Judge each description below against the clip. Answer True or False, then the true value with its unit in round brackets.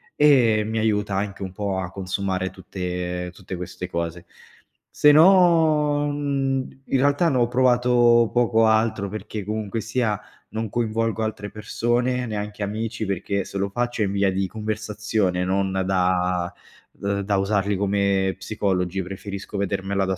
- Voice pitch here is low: True (105 Hz)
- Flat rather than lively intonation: False (3.6 semitones)